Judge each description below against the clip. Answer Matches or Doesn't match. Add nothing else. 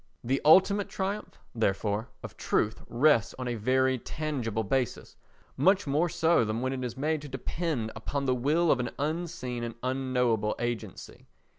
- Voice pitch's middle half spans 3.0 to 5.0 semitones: Matches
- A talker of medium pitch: Doesn't match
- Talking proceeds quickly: Doesn't match